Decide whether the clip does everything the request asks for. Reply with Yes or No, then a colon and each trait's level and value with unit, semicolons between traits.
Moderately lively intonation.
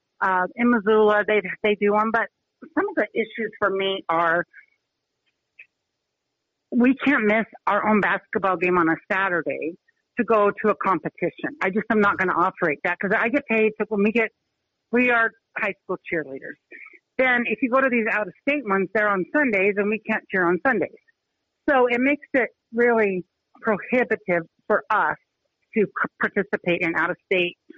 Yes: average, 3.5 semitones